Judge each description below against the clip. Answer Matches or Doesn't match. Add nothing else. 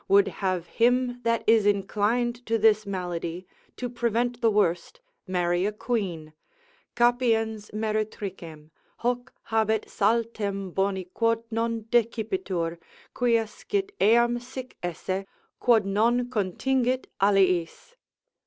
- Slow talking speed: Matches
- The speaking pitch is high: Matches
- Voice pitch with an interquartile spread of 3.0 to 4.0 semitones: Matches